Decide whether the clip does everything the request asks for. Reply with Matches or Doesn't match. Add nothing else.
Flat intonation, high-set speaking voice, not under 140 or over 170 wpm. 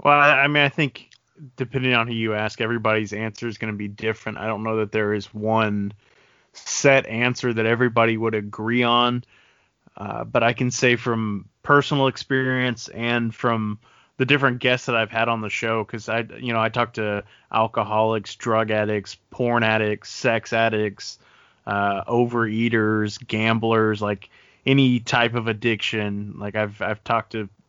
Doesn't match